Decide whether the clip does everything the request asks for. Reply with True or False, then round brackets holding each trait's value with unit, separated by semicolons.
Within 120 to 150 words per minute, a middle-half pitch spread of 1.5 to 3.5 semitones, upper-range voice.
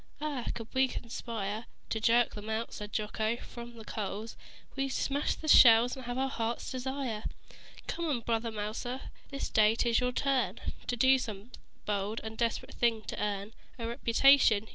False (165 wpm; 2.9 semitones; 230 Hz)